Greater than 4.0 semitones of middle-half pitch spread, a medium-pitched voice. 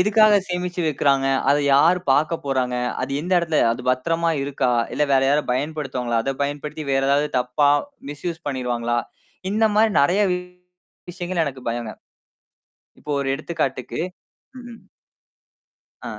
Yes: average, 4.7 semitones; medium, 145 Hz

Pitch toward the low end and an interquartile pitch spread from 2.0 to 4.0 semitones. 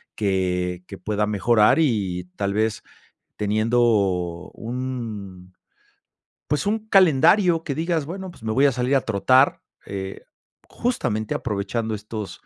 No: low, 110 Hz; average, 5.3 semitones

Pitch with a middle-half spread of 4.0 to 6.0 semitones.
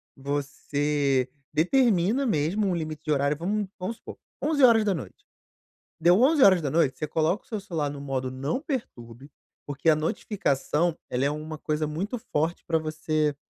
Yes: average, 5.3 semitones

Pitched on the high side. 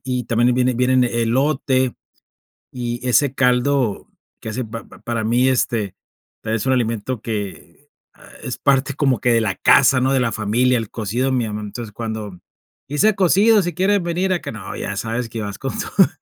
No: low, 125 Hz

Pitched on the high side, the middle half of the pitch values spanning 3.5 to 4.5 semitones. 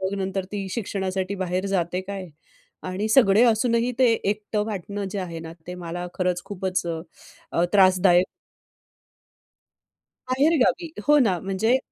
No: high, 195 Hz; average, 2.8 semitones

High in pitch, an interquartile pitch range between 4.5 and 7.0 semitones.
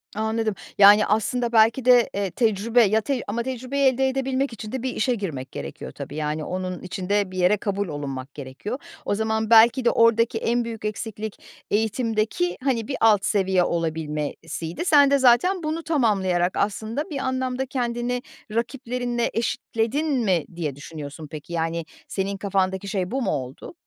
Yes: high, 220 Hz; average, 5.0 semitones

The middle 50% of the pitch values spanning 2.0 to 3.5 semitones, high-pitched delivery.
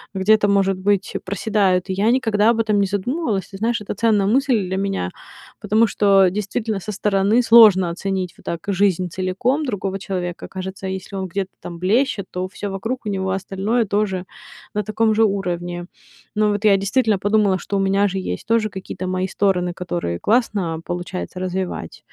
Yes: narrow, 2.4 semitones; high, 195 Hz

